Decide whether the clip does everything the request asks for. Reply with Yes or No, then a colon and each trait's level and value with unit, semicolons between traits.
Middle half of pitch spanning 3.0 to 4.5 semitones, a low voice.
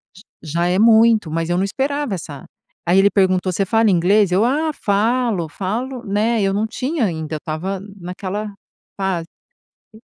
No: average, 4.1 semitones; high, 195 Hz